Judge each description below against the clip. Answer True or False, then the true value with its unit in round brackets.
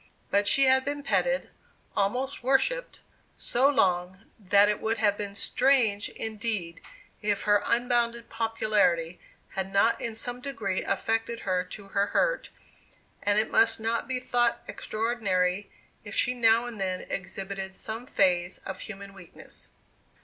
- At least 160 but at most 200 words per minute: False (140 wpm)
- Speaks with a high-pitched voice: True (215 Hz)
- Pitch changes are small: False (3.5 semitones)